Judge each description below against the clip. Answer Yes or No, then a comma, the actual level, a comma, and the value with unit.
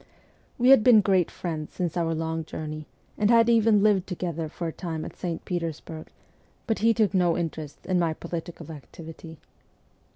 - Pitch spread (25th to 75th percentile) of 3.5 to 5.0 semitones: Yes, average, 4.1 semitones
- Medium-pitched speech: Yes, medium, 170 Hz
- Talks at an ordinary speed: Yes, average, 170 wpm